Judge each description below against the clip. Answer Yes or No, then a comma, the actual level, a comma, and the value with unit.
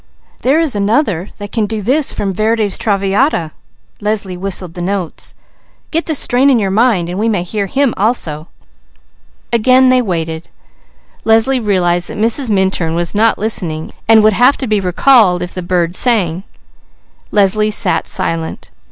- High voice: Yes, high, 205 Hz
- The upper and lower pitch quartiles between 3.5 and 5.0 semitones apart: Yes, average, 4.4 semitones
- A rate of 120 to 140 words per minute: Yes, slow, 135 wpm